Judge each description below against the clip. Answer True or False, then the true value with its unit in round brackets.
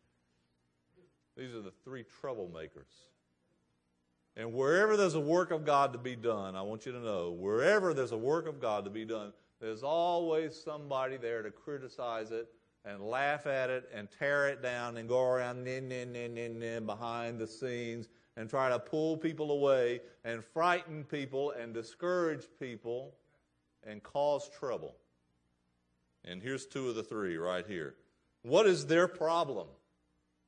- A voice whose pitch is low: True (120 Hz)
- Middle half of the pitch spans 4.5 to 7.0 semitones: True (5.4 semitones)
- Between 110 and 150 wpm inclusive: False (165 wpm)